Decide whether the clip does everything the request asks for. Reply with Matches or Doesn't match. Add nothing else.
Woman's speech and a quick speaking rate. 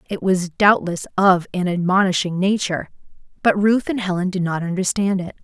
Doesn't match